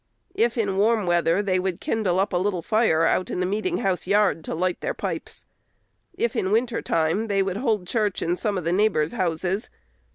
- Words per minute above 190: Yes, fast, 205 wpm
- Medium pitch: No, high, 195 Hz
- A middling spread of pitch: Yes, average, 3.2 semitones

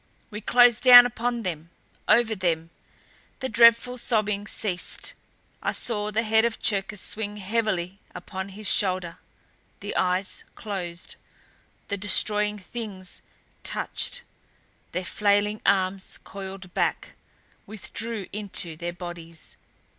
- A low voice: No, high, 205 Hz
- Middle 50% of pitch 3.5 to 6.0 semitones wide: No, average, 3.0 semitones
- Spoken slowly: Yes, slow, 115 wpm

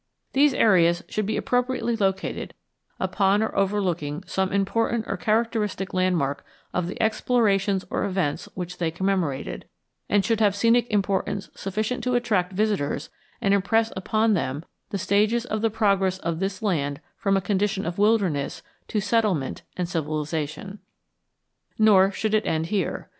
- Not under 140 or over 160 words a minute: Yes, average, 145 wpm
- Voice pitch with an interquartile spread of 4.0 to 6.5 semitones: No, average, 3.2 semitones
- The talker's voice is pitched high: Yes, high, 195 Hz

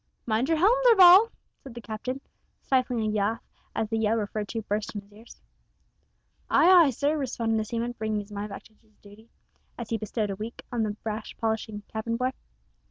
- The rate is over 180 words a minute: Yes, average, 200 wpm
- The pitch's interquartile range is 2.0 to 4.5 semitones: Yes, average, 2.9 semitones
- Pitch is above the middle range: Yes, high, 225 Hz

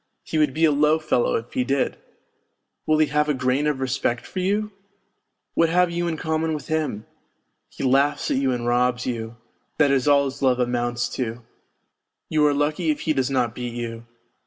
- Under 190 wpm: No, average, 200 wpm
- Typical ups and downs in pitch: Yes, average, 3.9 semitones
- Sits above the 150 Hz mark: No, medium, 140 Hz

